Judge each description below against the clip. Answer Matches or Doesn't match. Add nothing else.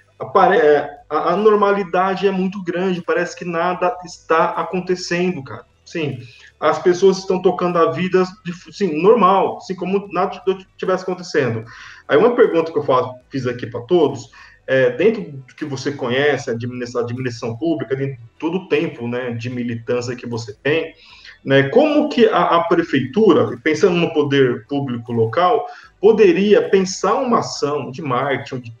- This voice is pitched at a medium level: Matches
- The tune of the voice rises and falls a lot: Matches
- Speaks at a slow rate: Doesn't match